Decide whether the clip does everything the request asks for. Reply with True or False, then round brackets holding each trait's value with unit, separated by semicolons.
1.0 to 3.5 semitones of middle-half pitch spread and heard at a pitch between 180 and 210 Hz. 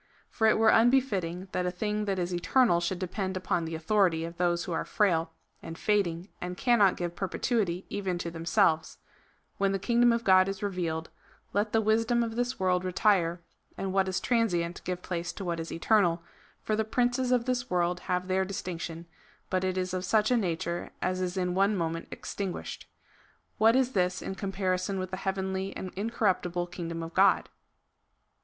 True (3.2 semitones; 185 Hz)